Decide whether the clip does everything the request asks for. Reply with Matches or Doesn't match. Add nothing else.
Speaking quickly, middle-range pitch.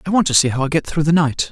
Matches